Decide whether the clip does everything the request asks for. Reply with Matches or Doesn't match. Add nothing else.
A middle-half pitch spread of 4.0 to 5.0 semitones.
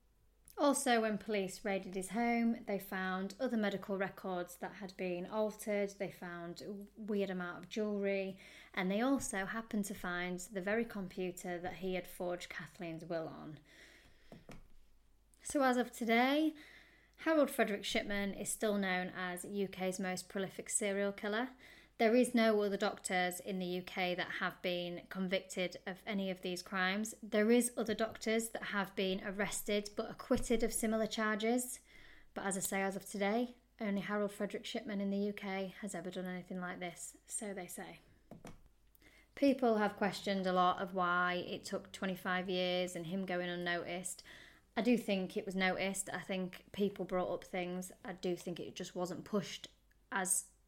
Doesn't match